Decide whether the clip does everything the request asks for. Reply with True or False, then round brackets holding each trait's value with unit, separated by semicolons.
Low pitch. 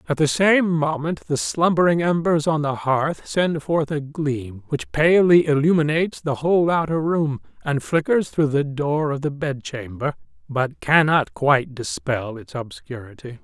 False (150 Hz)